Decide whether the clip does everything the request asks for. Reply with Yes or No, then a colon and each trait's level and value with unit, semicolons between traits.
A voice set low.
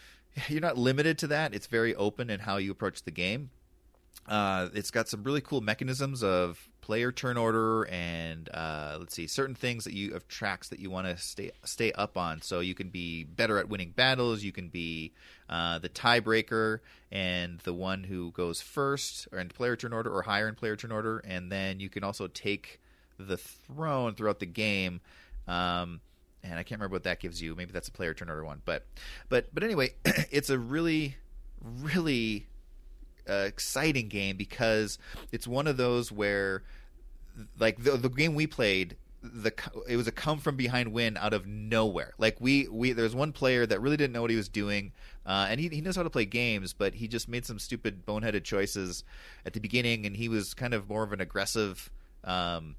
Yes: low, 105 Hz